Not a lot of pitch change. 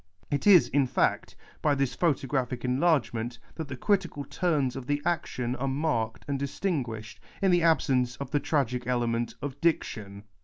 No: average, 4.2 semitones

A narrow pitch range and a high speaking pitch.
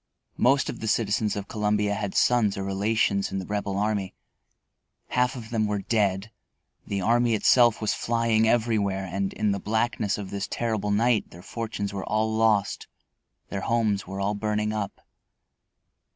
No: narrow, 2.1 semitones; low, 105 Hz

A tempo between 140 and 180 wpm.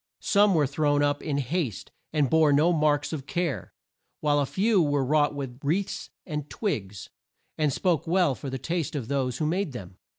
No: average, 190 wpm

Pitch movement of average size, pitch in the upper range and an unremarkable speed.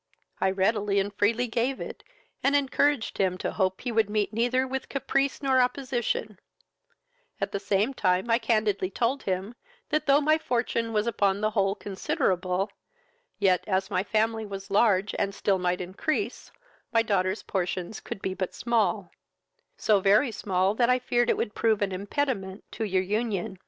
Yes: average, 3.7 semitones; high, 210 Hz; average, 170 wpm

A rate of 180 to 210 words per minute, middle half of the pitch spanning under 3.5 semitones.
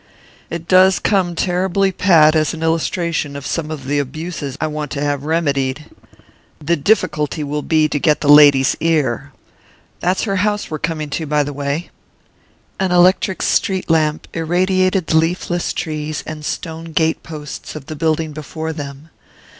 No: average, 160 wpm; average, 2.8 semitones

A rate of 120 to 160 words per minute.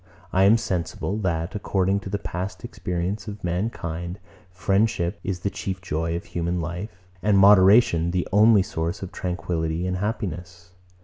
Yes: average, 150 wpm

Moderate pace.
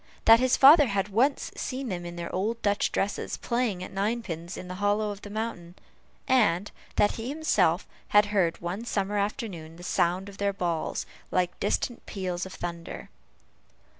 Yes: average, 170 wpm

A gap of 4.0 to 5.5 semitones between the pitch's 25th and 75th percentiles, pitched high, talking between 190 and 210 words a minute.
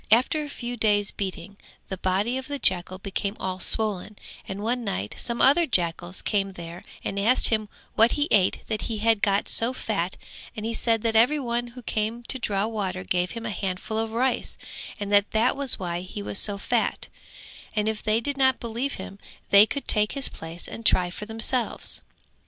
No: average, 3.3 semitones; high, 215 Hz; average, 200 wpm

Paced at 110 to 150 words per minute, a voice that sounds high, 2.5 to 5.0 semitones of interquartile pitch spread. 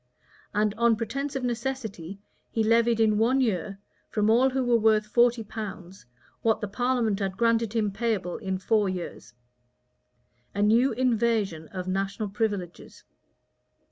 Yes: average, 140 wpm; high, 220 Hz; average, 3.0 semitones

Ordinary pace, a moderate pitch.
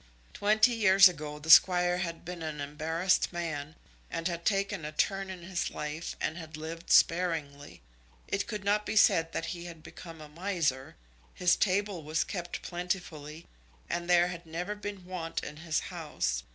Yes: average, 170 wpm; medium, 170 Hz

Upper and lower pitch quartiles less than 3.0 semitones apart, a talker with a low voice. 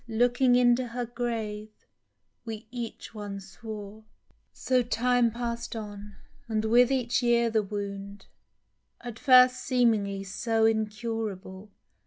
No: narrow, 2.5 semitones; high, 225 Hz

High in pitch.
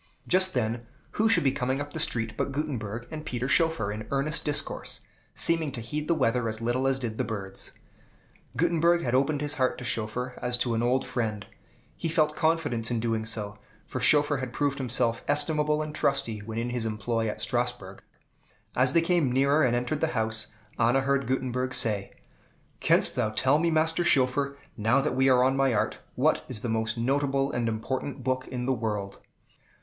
No: low, 130 Hz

